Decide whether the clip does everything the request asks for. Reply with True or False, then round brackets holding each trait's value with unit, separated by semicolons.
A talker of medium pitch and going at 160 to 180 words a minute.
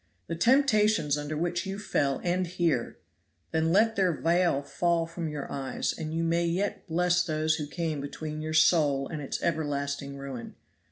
True (160 Hz; 170 wpm)